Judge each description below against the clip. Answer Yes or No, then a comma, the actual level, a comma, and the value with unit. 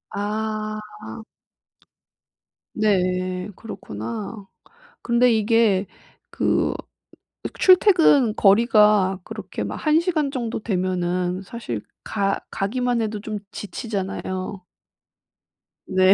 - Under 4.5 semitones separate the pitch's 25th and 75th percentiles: Yes, average, 3.7 semitones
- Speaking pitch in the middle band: No, high, 210 Hz